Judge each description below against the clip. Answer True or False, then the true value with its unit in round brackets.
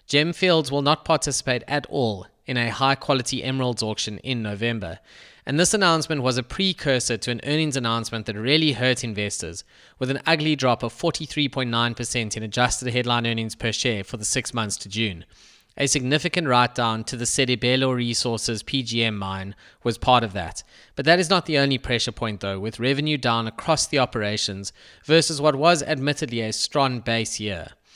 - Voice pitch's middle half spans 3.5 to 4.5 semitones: True (4.0 semitones)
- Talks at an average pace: True (180 wpm)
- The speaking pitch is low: True (125 Hz)